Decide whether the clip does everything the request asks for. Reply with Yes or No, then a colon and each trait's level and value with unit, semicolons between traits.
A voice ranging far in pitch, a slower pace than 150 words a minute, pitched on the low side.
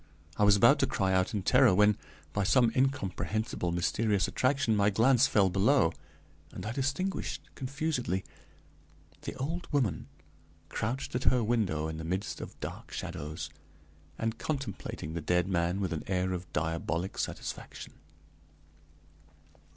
Yes: wide, 5.9 semitones; average, 140 wpm; low, 105 Hz